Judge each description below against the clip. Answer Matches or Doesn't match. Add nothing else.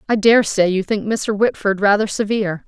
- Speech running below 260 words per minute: Matches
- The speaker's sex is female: Matches